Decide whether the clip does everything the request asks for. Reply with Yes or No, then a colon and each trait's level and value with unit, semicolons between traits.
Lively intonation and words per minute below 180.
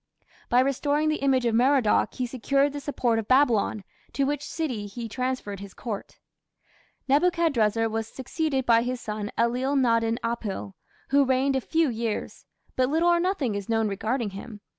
No: average, 3.7 semitones; average, 165 wpm